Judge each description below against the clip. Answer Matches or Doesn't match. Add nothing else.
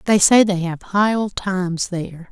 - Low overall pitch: Doesn't match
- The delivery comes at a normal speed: Doesn't match